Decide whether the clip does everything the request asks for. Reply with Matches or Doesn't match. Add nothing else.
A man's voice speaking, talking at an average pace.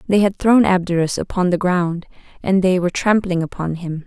Doesn't match